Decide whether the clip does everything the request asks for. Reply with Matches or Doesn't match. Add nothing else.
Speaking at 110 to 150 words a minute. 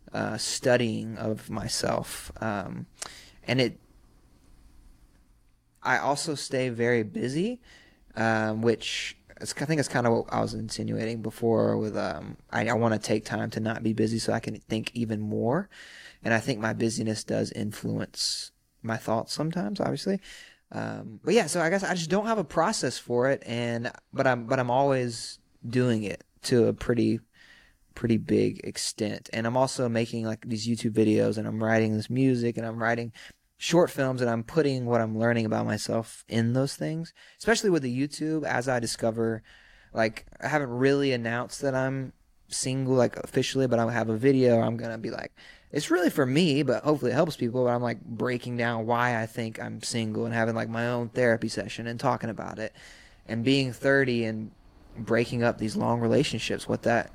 Doesn't match